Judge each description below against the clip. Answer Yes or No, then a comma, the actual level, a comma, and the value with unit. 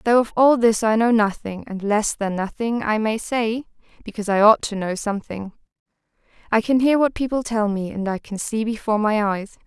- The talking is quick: Yes, fast, 210 wpm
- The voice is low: No, high, 220 Hz